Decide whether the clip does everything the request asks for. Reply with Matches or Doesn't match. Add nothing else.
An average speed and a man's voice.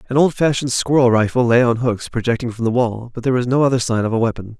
Doesn't match